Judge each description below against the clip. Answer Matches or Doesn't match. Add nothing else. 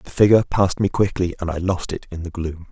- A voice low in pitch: Matches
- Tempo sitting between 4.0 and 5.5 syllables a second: Doesn't match